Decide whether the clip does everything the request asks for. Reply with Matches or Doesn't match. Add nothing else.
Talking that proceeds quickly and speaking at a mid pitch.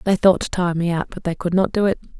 Matches